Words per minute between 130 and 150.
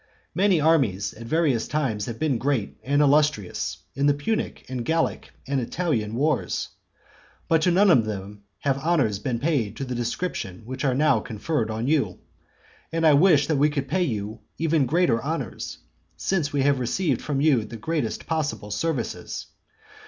No: average, 170 wpm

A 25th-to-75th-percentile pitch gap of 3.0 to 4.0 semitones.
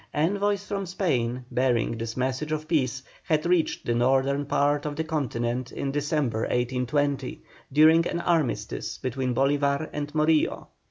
Yes: average, 3.6 semitones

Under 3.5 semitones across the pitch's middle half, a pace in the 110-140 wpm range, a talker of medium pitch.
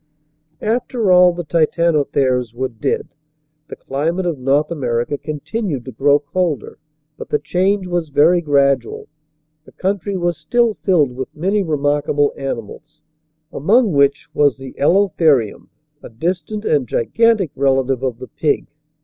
No: average, 4.9 semitones; slow, 135 wpm; medium, 150 Hz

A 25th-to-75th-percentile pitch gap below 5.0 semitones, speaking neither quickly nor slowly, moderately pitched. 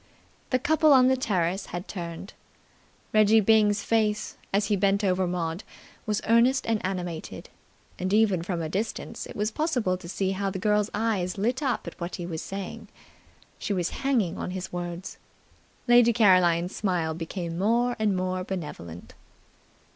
No: average, 3.7 semitones; average, 160 wpm; high, 195 Hz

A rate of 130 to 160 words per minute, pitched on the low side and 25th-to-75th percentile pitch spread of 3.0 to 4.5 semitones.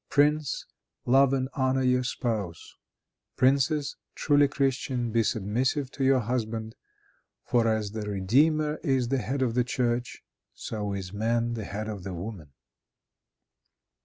Yes: slow, 135 wpm; low, 120 Hz; average, 3.7 semitones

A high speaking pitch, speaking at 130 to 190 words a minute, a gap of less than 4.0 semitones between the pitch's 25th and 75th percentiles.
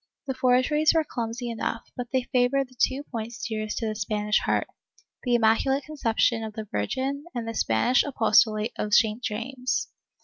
Yes: high, 240 Hz; average, 175 wpm; average, 3.0 semitones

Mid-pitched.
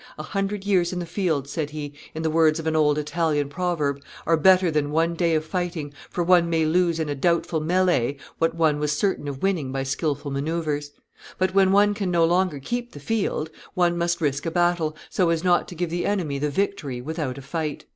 Yes: medium, 165 Hz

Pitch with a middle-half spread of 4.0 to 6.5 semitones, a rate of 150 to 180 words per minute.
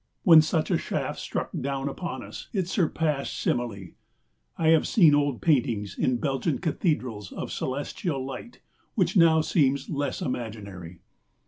No: average, 4.8 semitones; average, 140 wpm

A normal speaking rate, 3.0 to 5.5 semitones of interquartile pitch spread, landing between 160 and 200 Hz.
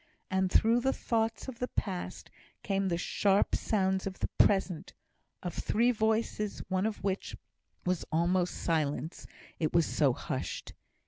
Yes: average, 145 wpm; average, 3.7 semitones; high, 190 Hz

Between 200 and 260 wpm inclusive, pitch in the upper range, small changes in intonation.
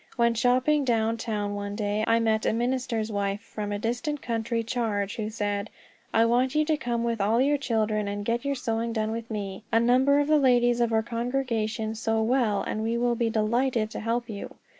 Yes: fast, 205 wpm; high, 230 Hz; narrow, 2.0 semitones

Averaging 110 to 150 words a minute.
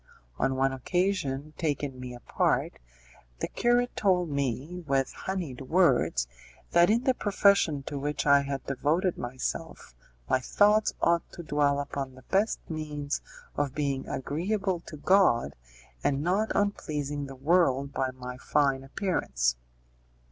Yes: average, 140 wpm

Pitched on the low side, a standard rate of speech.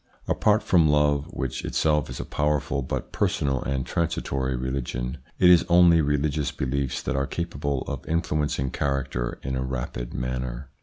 Yes: very low, 70 Hz; average, 155 wpm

